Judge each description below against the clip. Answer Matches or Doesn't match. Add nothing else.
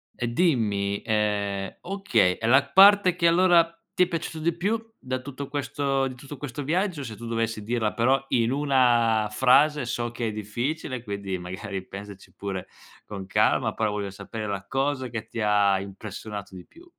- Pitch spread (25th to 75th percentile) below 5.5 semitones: Doesn't match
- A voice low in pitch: Matches